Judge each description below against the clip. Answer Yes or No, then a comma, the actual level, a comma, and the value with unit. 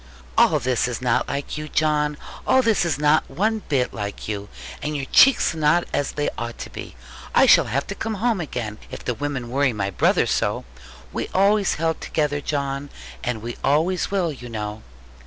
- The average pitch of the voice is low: No, medium, 145 Hz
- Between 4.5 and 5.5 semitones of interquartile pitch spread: Yes, average, 4.9 semitones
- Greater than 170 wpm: Yes, average, 195 wpm